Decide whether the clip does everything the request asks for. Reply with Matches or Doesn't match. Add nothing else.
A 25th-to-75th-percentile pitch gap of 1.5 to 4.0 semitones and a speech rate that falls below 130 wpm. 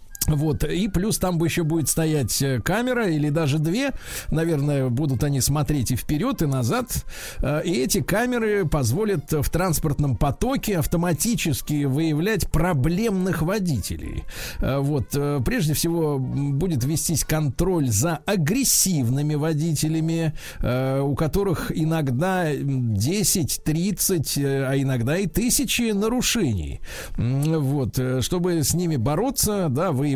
Doesn't match